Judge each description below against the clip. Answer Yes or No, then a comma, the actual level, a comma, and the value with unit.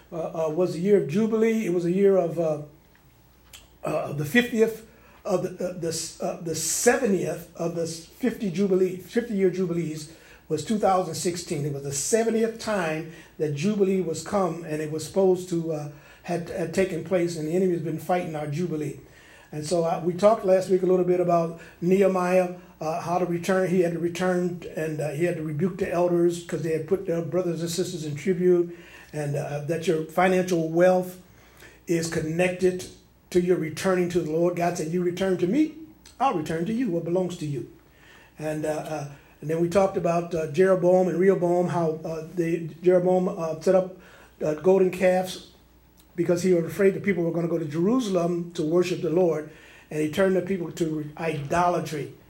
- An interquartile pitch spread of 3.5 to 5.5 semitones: No, narrow, 2.4 semitones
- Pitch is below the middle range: No, medium, 175 Hz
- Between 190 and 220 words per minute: Yes, average, 200 wpm